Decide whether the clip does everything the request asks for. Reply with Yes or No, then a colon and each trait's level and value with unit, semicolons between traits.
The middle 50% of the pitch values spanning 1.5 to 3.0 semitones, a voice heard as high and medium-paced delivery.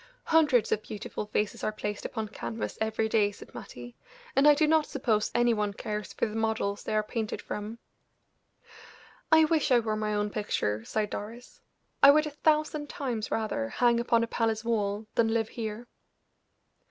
Yes: average, 2.7 semitones; high, 220 Hz; average, 175 wpm